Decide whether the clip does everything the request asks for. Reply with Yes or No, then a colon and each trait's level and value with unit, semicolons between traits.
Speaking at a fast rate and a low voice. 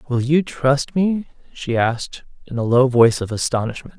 No: average, 180 wpm; low, 130 Hz